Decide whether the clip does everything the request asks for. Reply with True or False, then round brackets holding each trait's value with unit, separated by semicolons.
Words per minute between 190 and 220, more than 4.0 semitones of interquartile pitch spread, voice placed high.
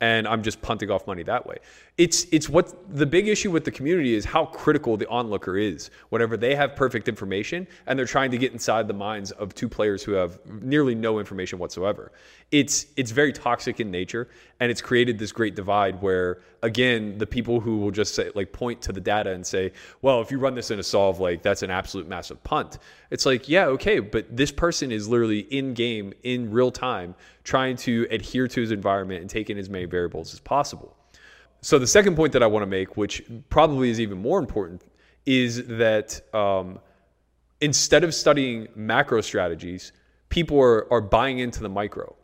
False (205 wpm; 4.6 semitones; 115 Hz)